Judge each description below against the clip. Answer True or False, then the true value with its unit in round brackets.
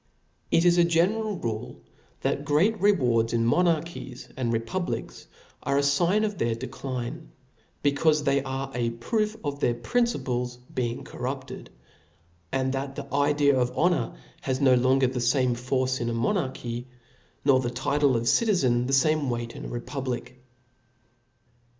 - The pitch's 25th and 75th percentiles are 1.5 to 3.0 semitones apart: False (4.3 semitones)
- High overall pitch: False (135 Hz)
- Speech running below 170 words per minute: True (150 wpm)